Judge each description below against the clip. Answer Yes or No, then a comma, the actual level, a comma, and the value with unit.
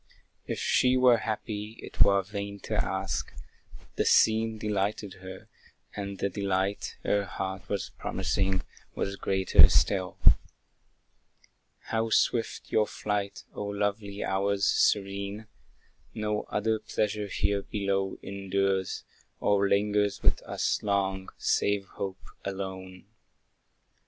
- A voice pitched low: Yes, low, 100 Hz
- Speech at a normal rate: No, slow, 110 wpm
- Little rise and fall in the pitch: Yes, narrow, 1.4 semitones